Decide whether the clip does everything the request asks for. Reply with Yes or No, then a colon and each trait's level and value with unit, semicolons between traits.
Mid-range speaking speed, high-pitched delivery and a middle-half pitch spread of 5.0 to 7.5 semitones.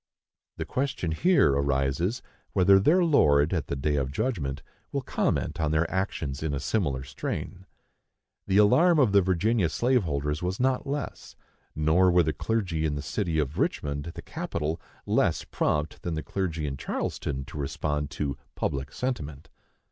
No: average, 165 wpm; very low, 80 Hz; wide, 5.4 semitones